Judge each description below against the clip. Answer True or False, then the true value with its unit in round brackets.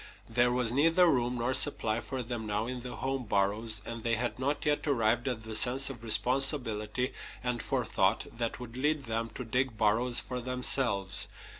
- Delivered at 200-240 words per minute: False (180 wpm)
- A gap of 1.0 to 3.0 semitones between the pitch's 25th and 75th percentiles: True (2.5 semitones)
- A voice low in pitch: True (120 Hz)